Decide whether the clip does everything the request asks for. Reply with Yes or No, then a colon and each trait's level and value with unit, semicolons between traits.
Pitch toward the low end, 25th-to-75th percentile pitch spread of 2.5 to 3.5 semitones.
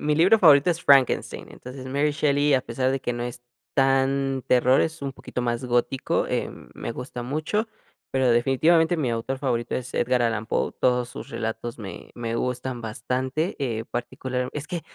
Yes: low, 130 Hz; average, 2.8 semitones